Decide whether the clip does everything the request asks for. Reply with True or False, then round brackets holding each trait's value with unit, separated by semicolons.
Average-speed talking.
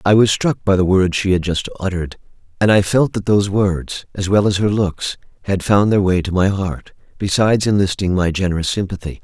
False (215 wpm)